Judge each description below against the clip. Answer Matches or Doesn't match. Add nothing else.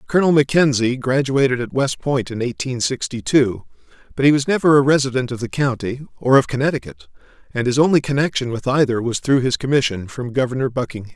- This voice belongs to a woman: Doesn't match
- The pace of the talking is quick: Doesn't match